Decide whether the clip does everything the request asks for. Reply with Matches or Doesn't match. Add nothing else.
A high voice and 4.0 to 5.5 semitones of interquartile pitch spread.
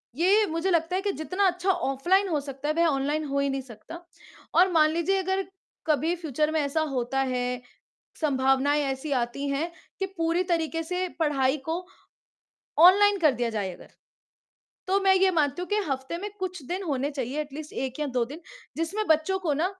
Matches